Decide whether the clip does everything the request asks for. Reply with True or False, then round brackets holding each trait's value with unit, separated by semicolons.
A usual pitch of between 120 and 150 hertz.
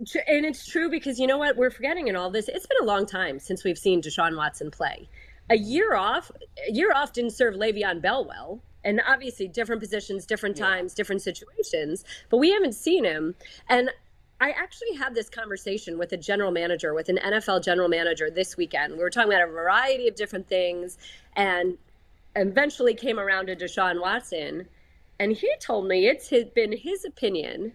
False (215 Hz)